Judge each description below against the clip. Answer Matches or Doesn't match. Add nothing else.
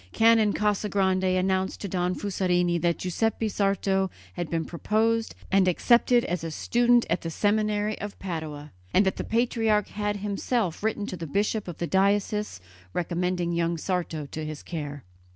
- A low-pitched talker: Doesn't match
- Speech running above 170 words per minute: Doesn't match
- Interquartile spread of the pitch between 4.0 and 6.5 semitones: Doesn't match